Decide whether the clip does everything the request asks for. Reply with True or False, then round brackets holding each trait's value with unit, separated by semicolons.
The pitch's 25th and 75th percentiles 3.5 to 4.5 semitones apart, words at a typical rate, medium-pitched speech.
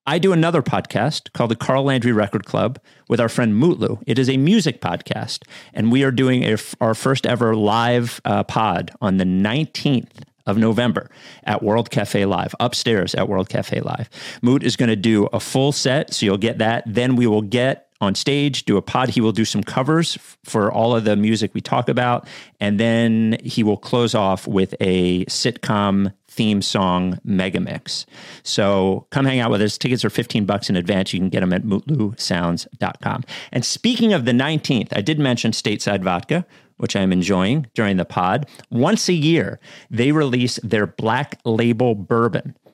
False (4.2 semitones; 190 wpm; 115 Hz)